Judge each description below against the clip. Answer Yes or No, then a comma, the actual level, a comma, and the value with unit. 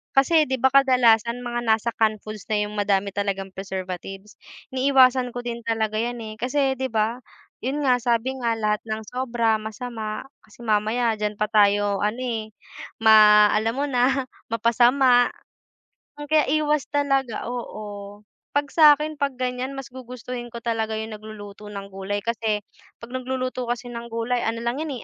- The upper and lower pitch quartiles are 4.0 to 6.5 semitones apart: No, average, 3.1 semitones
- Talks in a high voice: Yes, high, 235 Hz